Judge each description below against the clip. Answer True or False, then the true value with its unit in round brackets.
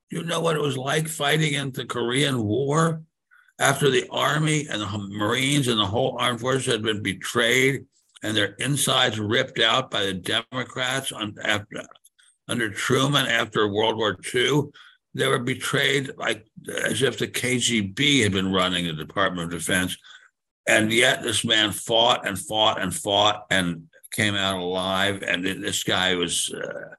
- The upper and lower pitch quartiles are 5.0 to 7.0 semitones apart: True (5.6 semitones)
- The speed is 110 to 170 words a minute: True (165 wpm)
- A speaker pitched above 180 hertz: False (120 Hz)